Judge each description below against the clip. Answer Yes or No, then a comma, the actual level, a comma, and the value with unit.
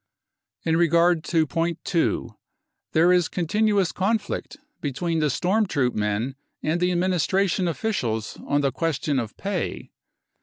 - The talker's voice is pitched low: No, medium, 170 Hz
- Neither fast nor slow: Yes, average, 150 wpm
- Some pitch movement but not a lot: Yes, average, 4.1 semitones